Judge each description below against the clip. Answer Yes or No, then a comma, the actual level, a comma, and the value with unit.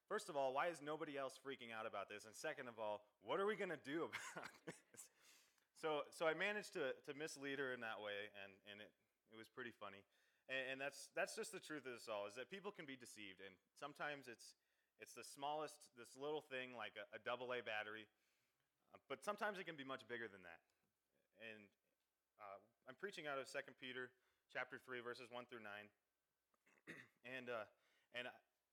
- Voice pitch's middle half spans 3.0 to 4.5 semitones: No, wide, 5.5 semitones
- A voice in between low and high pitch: No, low, 130 Hz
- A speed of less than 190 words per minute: No, fast, 205 wpm